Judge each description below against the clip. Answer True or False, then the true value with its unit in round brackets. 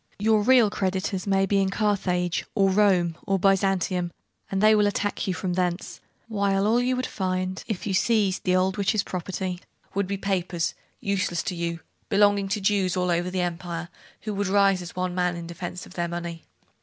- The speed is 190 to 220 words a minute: True (195 wpm)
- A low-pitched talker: False (190 Hz)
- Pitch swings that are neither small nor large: False (2.1 semitones)